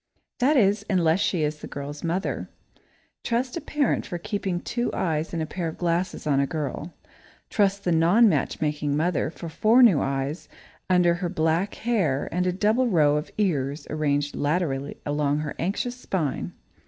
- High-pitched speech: No, medium, 170 Hz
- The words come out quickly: No, average, 170 wpm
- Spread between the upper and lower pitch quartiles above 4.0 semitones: Yes, average, 5.0 semitones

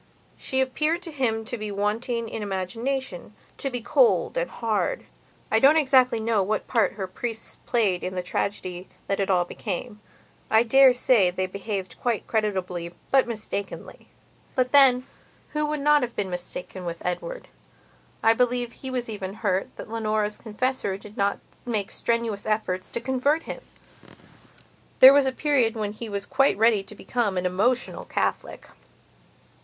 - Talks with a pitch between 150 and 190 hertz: No, high, 225 Hz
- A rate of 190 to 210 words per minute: No, average, 160 wpm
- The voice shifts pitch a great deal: No, average, 4.4 semitones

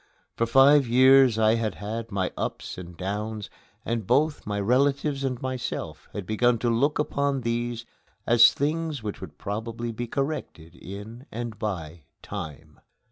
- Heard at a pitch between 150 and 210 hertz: No, low, 115 Hz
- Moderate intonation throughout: Yes, average, 4.3 semitones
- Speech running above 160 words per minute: No, average, 150 wpm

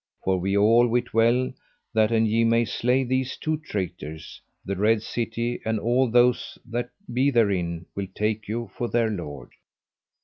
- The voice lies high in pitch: No, low, 115 Hz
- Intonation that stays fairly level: No, average, 3.0 semitones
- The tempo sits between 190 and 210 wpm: No, average, 165 wpm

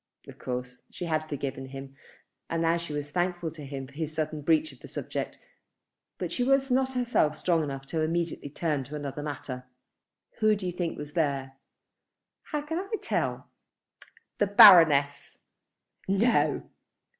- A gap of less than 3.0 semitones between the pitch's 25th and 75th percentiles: No, average, 4.1 semitones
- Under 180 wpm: Yes, average, 160 wpm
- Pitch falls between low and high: Yes, medium, 155 Hz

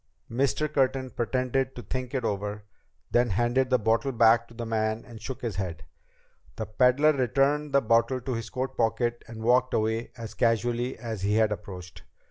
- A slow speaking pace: No, average, 185 wpm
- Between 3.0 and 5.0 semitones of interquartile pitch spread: No, narrow, 2.5 semitones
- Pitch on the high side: No, low, 120 Hz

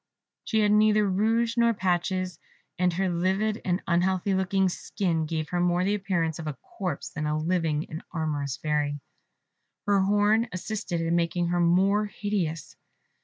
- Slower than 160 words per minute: No, average, 165 wpm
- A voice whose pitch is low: No, medium, 180 Hz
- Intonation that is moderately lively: Yes, average, 3.6 semitones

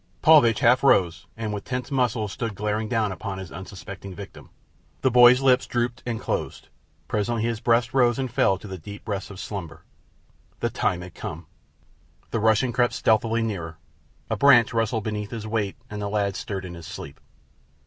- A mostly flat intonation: No, average, 3.3 semitones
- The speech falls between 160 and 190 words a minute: Yes, average, 180 wpm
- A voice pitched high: No, low, 110 Hz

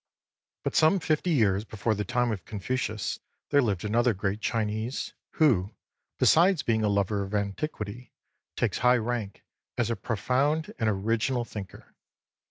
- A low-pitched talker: Yes, low, 110 Hz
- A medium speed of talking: Yes, average, 145 wpm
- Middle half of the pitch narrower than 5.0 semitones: Yes, average, 3.7 semitones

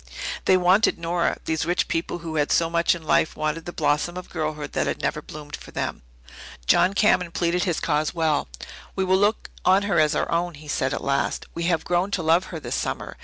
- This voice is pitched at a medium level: Yes, medium, 170 Hz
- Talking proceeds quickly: Yes, fast, 220 wpm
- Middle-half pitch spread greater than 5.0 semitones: No, narrow, 2.6 semitones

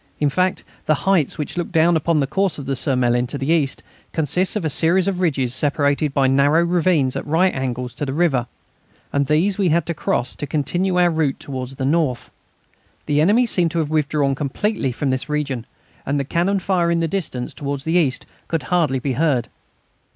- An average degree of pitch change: Yes, average, 4.1 semitones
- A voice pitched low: No, medium, 150 Hz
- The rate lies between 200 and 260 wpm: Yes, fast, 205 wpm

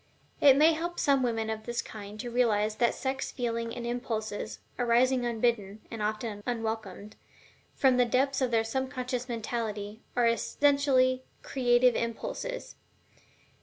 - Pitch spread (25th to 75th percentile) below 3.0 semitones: Yes, narrow, 2.6 semitones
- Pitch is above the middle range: Yes, high, 240 Hz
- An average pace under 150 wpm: Yes, average, 140 wpm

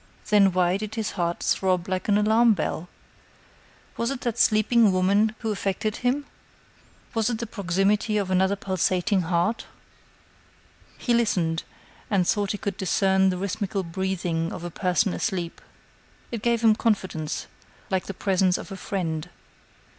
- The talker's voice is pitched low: No, high, 195 Hz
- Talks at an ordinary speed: Yes, average, 150 wpm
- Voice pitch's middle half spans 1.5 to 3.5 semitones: Yes, average, 2.9 semitones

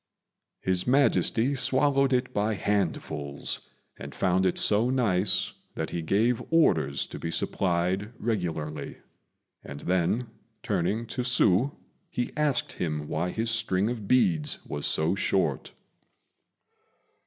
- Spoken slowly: Yes, slow, 120 wpm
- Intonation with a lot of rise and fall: Yes, wide, 6.1 semitones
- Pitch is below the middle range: Yes, low, 100 Hz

